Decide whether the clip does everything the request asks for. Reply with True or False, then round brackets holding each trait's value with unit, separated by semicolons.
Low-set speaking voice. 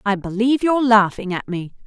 False (215 Hz)